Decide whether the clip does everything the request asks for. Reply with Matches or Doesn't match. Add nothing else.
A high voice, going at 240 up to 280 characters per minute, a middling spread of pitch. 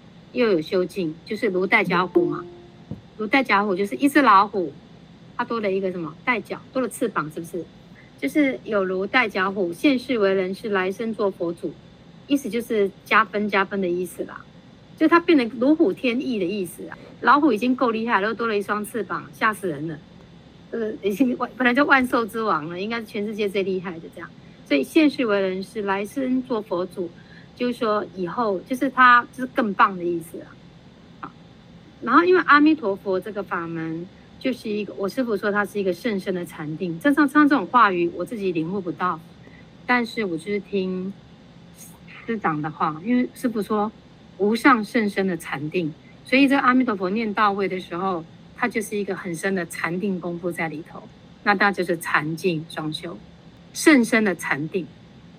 Matches